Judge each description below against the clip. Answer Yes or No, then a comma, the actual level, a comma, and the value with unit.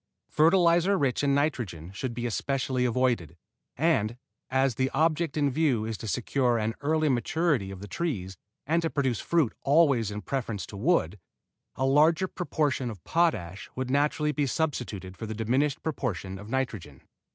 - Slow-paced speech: No, average, 165 wpm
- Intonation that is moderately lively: No, wide, 5.8 semitones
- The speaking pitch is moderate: No, low, 130 Hz